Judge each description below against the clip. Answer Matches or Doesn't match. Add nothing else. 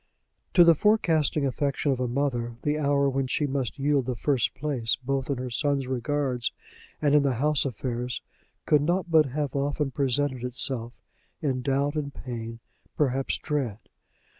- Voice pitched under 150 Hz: Matches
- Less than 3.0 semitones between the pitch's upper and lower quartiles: Matches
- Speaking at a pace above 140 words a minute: Matches